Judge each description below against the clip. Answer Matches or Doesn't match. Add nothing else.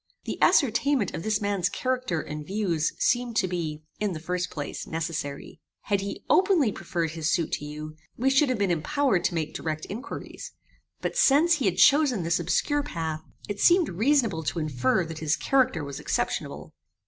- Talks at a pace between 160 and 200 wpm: Matches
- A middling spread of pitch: Doesn't match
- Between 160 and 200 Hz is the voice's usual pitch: Matches